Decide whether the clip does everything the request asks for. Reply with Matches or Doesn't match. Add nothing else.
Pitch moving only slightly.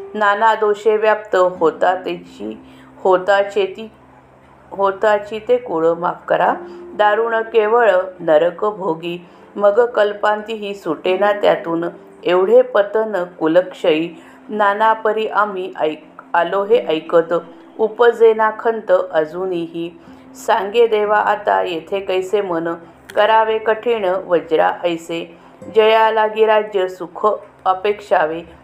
Doesn't match